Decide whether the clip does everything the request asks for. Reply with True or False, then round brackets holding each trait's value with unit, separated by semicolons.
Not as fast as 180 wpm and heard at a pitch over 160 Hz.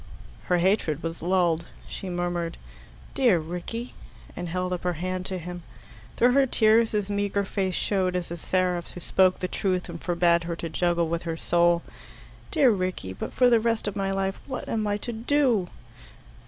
False (185 wpm; 185 Hz)